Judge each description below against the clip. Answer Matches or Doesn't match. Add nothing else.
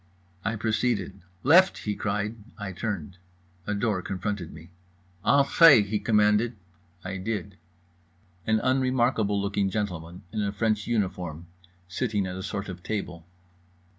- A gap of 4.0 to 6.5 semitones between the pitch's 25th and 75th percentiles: Doesn't match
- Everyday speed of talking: Doesn't match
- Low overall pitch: Matches